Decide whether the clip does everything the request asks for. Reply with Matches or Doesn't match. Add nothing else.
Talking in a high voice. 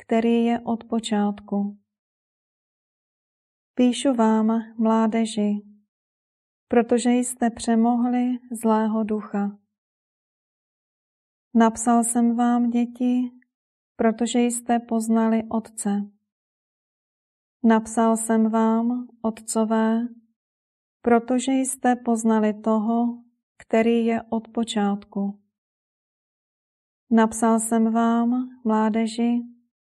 Matches